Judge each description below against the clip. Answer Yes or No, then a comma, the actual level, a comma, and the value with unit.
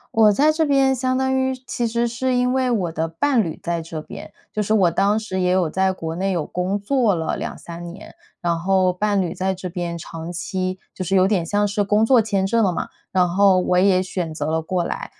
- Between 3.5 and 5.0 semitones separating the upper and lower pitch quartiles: Yes, average, 3.9 semitones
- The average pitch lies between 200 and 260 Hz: No, high, 190 Hz